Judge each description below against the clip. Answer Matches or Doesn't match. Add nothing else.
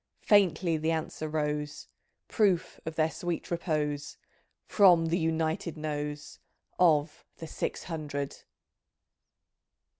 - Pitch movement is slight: Matches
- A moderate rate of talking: Doesn't match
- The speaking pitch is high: Doesn't match